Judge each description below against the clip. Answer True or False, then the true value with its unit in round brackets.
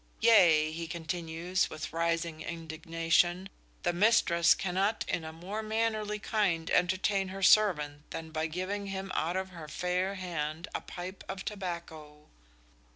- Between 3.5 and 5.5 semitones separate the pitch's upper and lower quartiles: False (2.9 semitones)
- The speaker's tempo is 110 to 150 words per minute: True (140 wpm)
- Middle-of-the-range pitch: True (175 Hz)